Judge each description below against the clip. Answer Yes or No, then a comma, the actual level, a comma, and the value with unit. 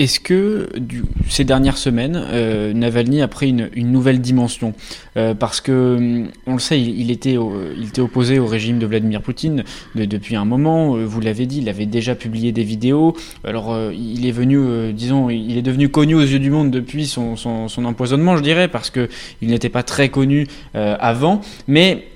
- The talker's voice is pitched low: Yes, low, 125 Hz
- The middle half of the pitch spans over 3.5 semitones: No, average, 3.2 semitones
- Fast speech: No, average, 205 wpm